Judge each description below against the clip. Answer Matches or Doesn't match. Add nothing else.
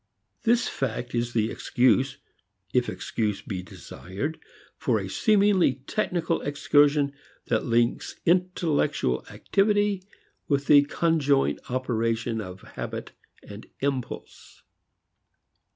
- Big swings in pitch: Matches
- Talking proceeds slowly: Matches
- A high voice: Doesn't match